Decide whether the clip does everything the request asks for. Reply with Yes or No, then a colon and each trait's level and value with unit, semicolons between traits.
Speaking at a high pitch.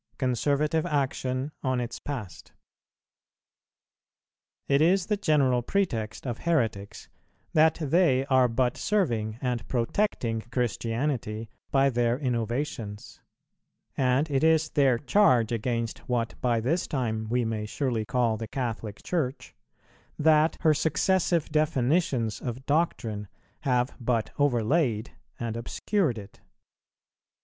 No: low, 125 Hz